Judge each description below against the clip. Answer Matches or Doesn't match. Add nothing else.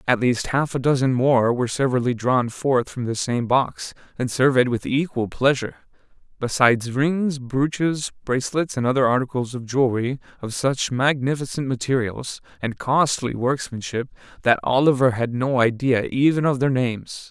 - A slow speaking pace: Doesn't match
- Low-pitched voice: Matches